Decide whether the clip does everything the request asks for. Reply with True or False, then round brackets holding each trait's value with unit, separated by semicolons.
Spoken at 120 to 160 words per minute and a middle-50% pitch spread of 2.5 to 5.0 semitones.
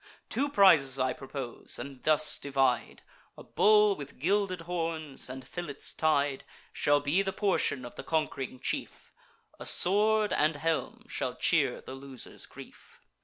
False (145 wpm; 5.4 semitones)